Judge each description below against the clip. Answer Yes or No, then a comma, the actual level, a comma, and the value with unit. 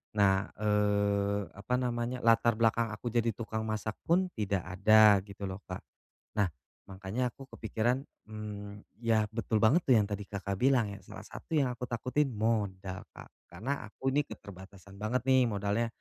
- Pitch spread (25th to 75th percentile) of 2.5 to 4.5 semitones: Yes, average, 2.8 semitones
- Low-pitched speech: Yes, low, 110 Hz